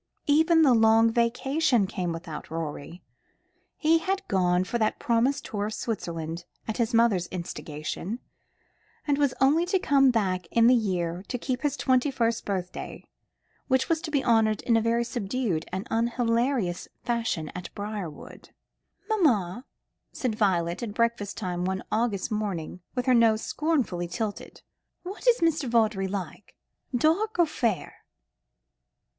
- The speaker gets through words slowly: No, average, 150 wpm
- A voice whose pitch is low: No, high, 230 Hz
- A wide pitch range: Yes, wide, 5.8 semitones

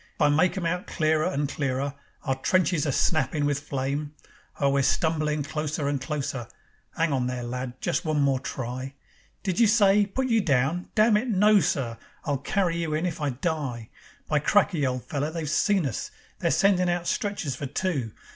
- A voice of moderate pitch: Yes, medium, 150 Hz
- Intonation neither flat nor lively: Yes, average, 4.6 semitones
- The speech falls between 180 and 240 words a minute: Yes, average, 185 wpm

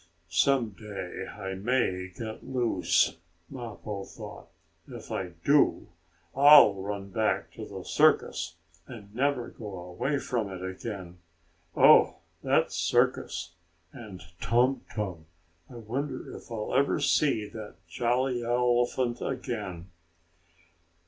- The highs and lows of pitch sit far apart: No, average, 4.5 semitones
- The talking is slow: Yes, slow, 115 wpm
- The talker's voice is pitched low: Yes, low, 110 Hz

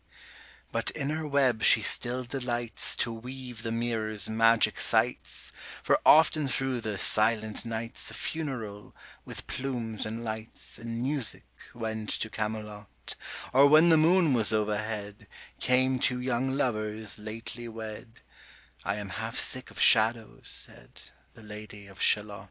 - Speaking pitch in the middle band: No, low, 115 Hz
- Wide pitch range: No, average, 3.0 semitones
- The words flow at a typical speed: Yes, average, 145 wpm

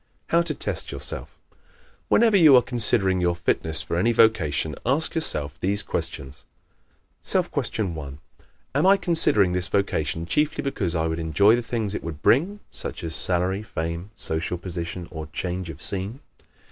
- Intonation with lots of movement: Yes, wide, 6.3 semitones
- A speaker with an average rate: Yes, average, 165 wpm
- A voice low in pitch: Yes, very low, 95 Hz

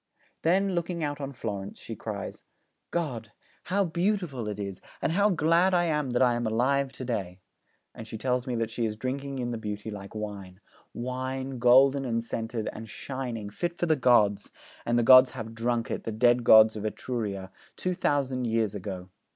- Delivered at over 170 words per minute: Yes, average, 190 wpm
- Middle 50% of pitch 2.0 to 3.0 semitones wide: No, average, 4.1 semitones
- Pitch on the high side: No, low, 120 Hz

